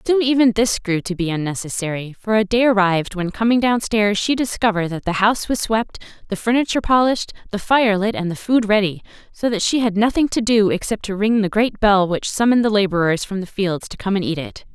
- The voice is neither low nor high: No, high, 210 Hz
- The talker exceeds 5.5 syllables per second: Yes, 5.9 syllables/s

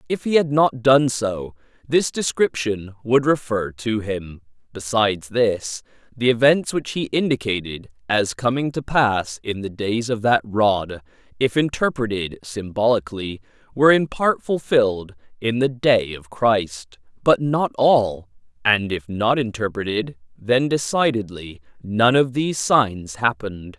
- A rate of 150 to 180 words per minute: No, average, 140 wpm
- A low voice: Yes, low, 115 Hz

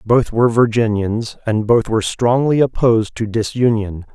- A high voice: No, low, 115 Hz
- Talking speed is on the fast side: No, average, 145 wpm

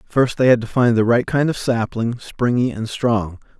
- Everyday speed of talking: No, fast, 215 wpm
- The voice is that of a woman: No, male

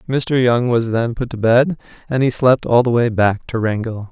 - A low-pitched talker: Yes, low, 120 Hz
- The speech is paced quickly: Yes, fast, 235 wpm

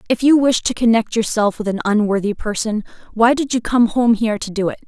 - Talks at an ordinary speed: No, fast, 235 wpm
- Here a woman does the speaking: Yes, female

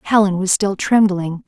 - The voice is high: Yes, high, 195 Hz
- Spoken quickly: No, average, 165 wpm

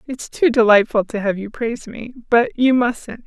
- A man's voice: No, female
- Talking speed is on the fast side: No, average, 185 wpm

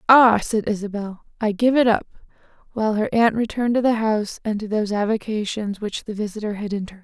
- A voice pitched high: Yes, high, 215 Hz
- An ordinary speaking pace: Yes, average, 190 wpm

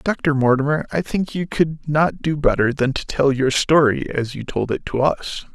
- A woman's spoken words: No, male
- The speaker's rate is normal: No, fast, 215 wpm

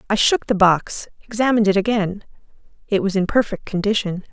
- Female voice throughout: Yes, female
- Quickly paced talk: No, average, 165 wpm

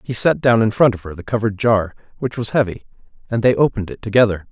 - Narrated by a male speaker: Yes, male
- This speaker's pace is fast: Yes, fast, 215 wpm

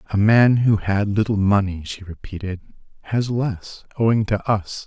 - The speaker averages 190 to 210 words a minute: No, average, 160 wpm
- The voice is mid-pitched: No, low, 105 Hz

